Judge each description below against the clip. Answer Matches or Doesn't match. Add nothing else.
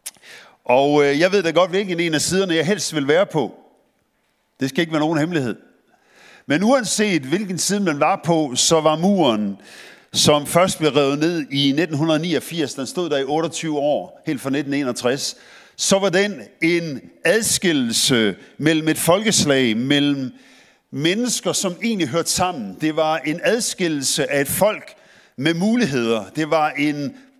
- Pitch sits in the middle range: Matches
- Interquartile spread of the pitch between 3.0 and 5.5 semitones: Matches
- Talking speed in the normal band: Matches